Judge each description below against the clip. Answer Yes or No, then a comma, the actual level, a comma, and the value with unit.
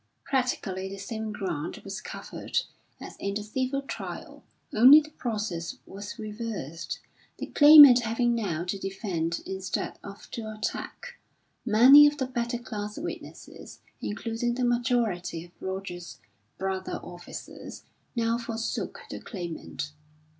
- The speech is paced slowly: Yes, slow, 125 wpm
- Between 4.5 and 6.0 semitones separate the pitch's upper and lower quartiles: No, average, 4.1 semitones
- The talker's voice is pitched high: Yes, high, 215 Hz